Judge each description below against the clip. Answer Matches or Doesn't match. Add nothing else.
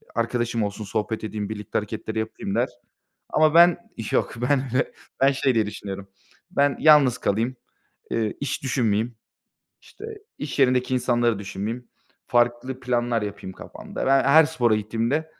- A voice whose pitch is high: Doesn't match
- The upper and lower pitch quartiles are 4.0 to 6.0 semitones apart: Doesn't match